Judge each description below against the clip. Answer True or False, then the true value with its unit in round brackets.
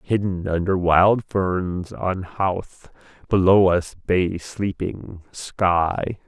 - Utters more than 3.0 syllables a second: False (2.7 syllables/s)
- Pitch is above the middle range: False (90 Hz)